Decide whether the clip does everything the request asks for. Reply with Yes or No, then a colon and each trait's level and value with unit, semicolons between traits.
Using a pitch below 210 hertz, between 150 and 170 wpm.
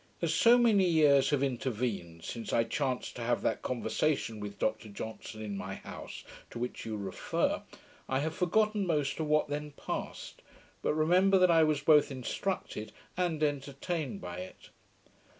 Yes: medium, 140 Hz; average, 165 wpm